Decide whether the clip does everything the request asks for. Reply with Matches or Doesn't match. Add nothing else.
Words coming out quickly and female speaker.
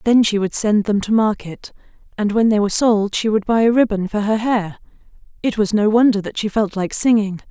Matches